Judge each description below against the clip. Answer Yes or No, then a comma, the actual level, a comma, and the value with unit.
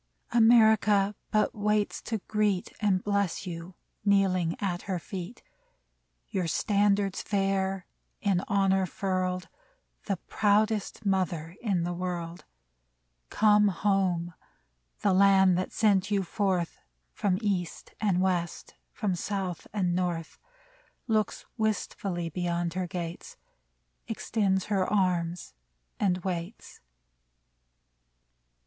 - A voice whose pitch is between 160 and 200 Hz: Yes, high, 190 Hz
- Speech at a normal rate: No, slow, 105 wpm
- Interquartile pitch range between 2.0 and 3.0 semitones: Yes, narrow, 2.5 semitones